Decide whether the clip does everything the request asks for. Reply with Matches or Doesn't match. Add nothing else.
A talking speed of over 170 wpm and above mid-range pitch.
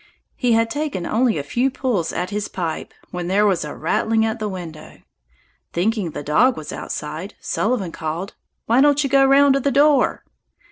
Matches